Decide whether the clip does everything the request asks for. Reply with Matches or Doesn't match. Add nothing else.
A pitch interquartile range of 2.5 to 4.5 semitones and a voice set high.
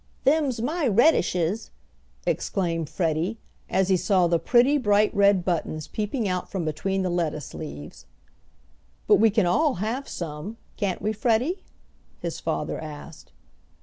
Doesn't match